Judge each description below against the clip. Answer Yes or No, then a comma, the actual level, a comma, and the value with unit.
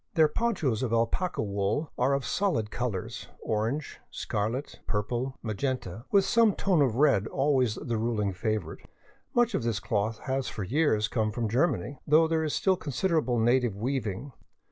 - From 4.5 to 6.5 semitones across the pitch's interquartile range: Yes, wide, 5.6 semitones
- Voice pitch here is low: Yes, low, 125 Hz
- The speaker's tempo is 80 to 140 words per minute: No, average, 170 wpm